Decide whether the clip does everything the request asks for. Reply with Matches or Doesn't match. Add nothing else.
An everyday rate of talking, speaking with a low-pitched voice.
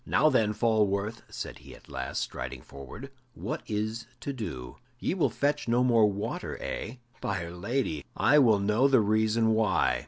Matches